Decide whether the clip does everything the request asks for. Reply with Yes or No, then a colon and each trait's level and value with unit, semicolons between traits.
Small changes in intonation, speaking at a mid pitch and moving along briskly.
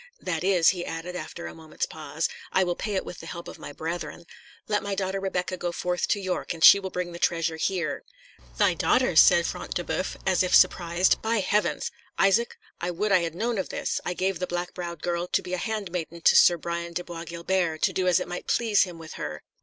Yes: narrow, 1.9 semitones; medium, 180 Hz; fast, 235 wpm